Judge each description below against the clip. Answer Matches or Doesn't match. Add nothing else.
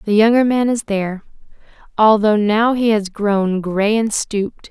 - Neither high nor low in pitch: Doesn't match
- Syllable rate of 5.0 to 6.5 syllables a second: Doesn't match